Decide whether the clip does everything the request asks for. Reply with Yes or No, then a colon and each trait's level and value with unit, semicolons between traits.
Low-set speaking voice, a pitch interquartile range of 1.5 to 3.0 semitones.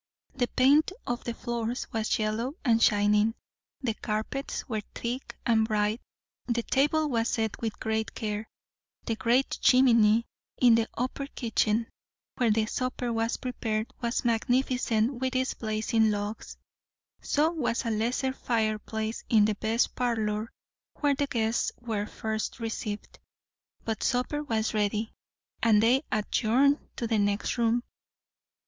No: high, 230 Hz; narrow, 2.4 semitones